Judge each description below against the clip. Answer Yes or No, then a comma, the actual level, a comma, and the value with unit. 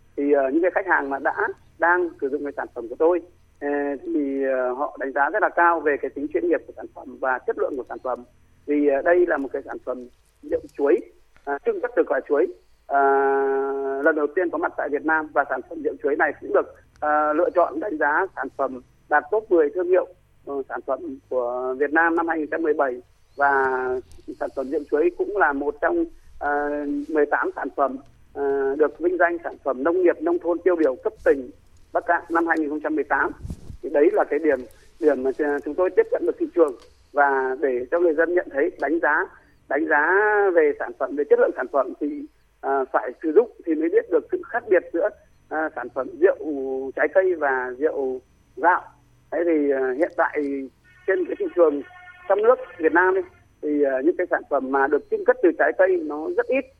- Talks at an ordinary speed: Yes, average, 220 wpm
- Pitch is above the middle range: No, medium, 165 Hz